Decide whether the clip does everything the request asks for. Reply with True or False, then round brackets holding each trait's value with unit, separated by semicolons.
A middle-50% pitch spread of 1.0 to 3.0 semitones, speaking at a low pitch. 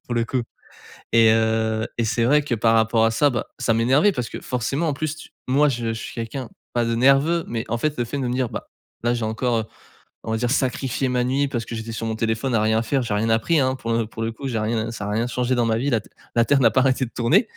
True (2.7 semitones; 120 Hz)